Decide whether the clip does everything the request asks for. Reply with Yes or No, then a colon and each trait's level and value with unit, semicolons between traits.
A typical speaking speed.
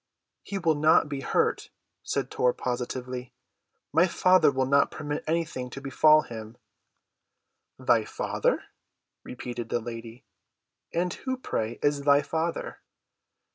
No: slow, 125 wpm